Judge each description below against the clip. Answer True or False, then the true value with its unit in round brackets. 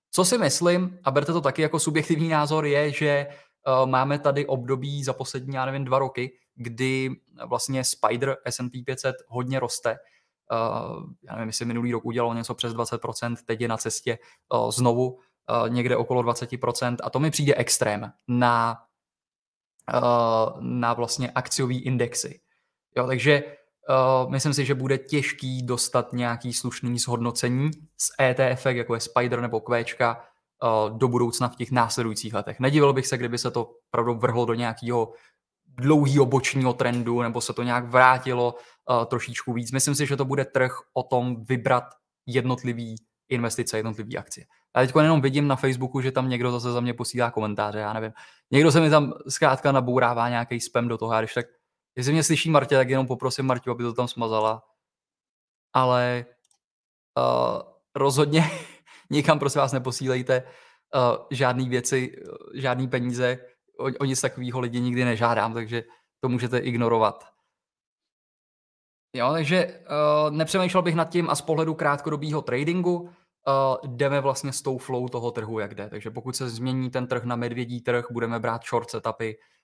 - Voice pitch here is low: True (125 Hz)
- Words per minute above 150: True (160 wpm)